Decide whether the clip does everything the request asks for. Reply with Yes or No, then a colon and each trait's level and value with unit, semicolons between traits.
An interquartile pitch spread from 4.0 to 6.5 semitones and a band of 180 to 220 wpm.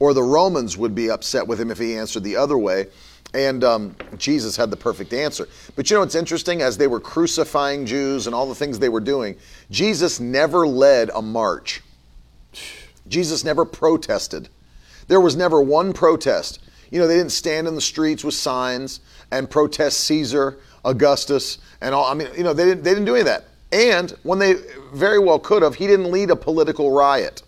Yes: average, 4.9 semitones; average, 200 wpm